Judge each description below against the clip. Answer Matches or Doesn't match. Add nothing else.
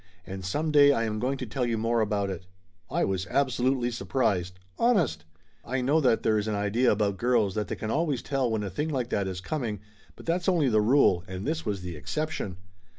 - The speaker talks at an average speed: Doesn't match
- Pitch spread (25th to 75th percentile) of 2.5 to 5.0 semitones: Doesn't match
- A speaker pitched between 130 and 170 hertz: Doesn't match